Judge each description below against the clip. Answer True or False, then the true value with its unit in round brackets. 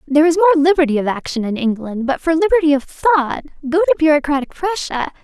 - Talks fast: False (195 wpm)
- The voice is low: False (300 Hz)